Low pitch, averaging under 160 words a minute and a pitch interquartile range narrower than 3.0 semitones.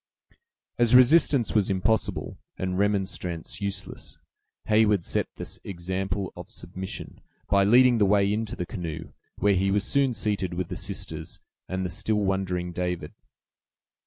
Yes: very low, 95 Hz; average, 140 wpm; narrow, 2.6 semitones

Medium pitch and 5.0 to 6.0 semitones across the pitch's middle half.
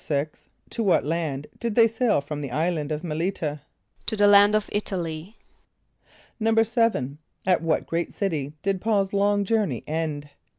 Yes: medium, 180 Hz; average, 5.3 semitones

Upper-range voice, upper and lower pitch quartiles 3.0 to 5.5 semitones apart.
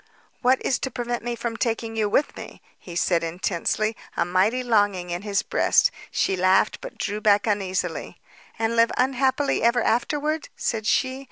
Yes: high, 225 Hz; average, 3.9 semitones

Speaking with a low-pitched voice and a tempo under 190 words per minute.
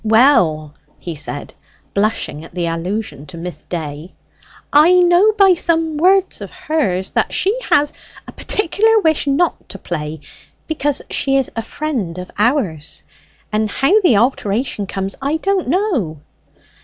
No: high, 245 Hz; average, 145 wpm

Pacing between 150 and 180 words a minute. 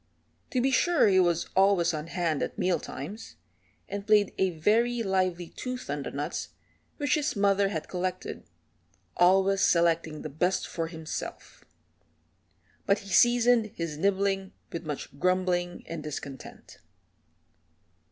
No: slow, 135 wpm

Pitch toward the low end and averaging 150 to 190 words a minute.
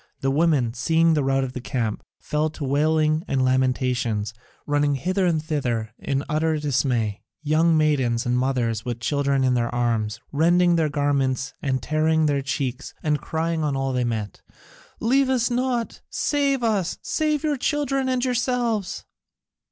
No: medium, 145 Hz; average, 160 wpm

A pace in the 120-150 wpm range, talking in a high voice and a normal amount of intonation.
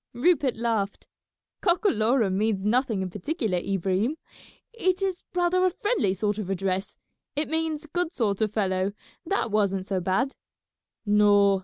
No: average, 140 wpm; high, 215 Hz; wide, 8.1 semitones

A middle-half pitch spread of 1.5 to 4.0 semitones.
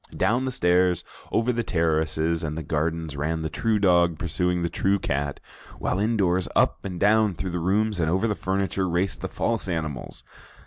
Yes: average, 3.4 semitones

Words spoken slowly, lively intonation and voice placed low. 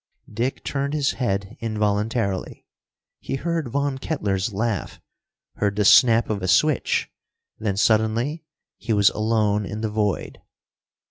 No: slow, 130 wpm; average, 4.1 semitones; low, 110 Hz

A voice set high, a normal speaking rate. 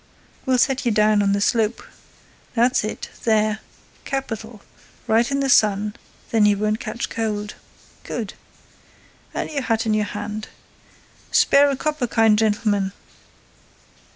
No: high, 220 Hz; slow, 115 wpm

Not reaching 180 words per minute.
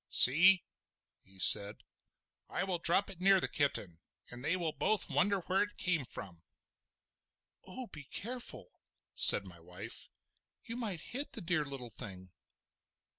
Yes: average, 145 wpm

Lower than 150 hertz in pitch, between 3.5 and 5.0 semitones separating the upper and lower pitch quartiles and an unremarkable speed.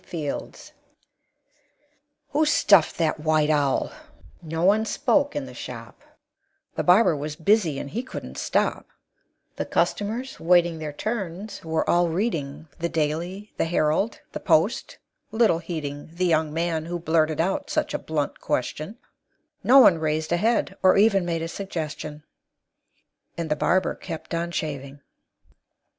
No: medium, 170 Hz; average, 4.2 semitones; average, 145 wpm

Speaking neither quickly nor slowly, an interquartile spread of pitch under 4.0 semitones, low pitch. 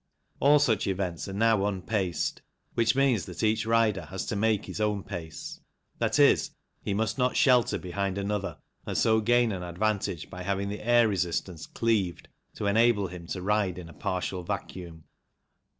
Yes: average, 165 wpm; average, 3.4 semitones; low, 100 Hz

